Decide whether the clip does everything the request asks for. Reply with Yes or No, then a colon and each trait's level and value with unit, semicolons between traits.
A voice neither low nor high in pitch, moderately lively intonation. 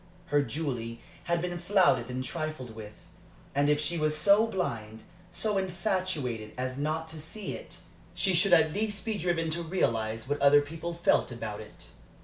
No: medium, 155 Hz; wide, 5.7 semitones